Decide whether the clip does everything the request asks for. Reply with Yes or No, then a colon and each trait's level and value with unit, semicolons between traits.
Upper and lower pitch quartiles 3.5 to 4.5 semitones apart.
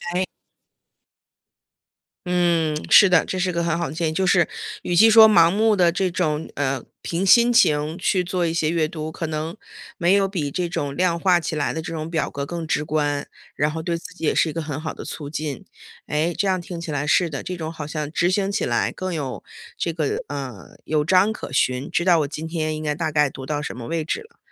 No: average, 2.9 semitones